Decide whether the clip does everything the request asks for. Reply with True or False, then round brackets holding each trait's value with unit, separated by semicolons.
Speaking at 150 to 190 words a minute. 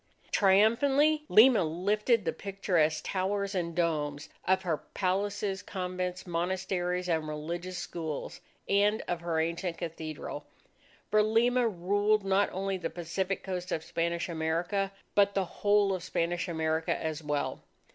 False (135 wpm)